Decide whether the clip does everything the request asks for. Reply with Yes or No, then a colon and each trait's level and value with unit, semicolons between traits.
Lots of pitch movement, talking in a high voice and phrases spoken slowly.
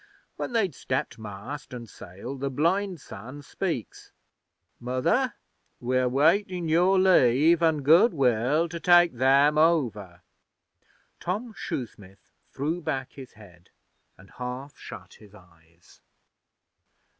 No: wide, 6.2 semitones; medium, 140 Hz; slow, 115 wpm